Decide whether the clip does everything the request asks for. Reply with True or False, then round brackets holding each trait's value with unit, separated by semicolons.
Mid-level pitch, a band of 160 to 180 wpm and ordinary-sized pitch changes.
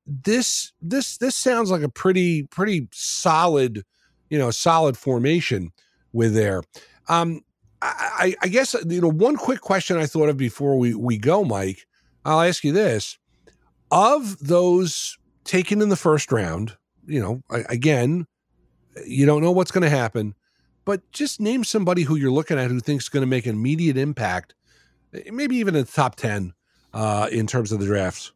False (150 Hz; 165 wpm; 7.9 semitones)